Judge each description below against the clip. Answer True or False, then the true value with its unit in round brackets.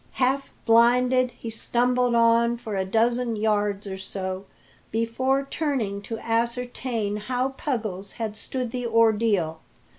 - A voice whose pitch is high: True (230 Hz)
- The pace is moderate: False (125 wpm)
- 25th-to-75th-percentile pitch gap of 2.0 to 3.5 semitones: True (3.0 semitones)